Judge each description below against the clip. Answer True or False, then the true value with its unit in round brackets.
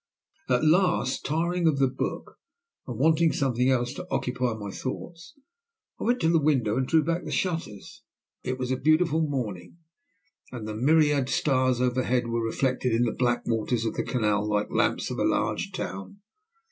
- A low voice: True (130 Hz)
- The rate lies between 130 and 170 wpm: False (180 wpm)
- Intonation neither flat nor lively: True (5.0 semitones)